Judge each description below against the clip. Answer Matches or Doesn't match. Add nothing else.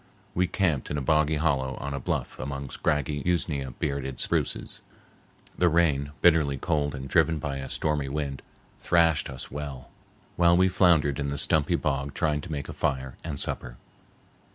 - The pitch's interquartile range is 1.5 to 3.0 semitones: Matches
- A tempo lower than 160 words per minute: Doesn't match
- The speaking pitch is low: Matches